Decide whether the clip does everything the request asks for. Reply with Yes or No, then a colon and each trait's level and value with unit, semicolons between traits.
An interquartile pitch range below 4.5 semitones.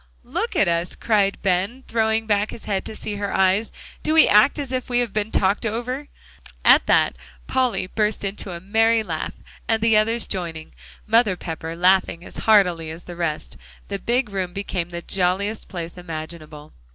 Yes: average, 4.1 semitones